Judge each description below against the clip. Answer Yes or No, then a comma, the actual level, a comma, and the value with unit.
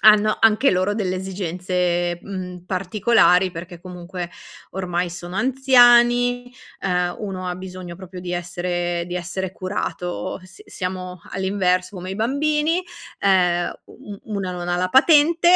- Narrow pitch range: No, average, 3.1 semitones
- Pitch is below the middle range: No, medium, 185 Hz